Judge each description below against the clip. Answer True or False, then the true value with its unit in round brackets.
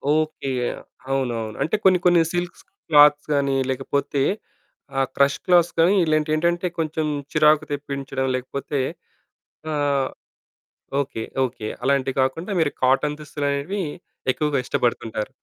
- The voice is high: False (145 Hz)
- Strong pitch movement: False (2.6 semitones)